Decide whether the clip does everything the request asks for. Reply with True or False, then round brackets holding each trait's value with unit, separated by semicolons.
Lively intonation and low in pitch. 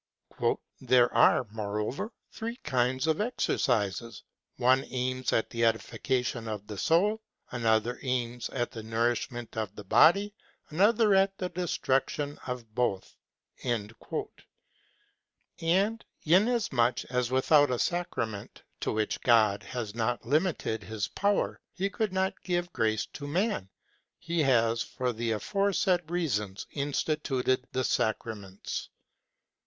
True (7.3 semitones; 125 Hz)